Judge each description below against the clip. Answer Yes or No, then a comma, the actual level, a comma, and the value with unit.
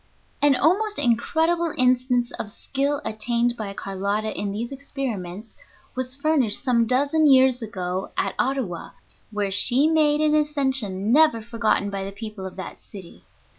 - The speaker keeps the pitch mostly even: No, wide, 5.4 semitones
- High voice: Yes, high, 245 Hz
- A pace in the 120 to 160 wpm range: Yes, average, 150 wpm